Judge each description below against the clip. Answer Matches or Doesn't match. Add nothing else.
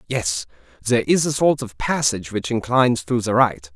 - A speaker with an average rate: Matches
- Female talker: Doesn't match